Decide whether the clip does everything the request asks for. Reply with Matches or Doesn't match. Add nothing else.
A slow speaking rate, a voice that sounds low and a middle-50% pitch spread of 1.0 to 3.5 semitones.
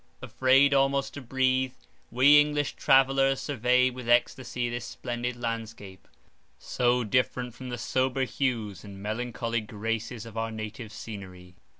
Matches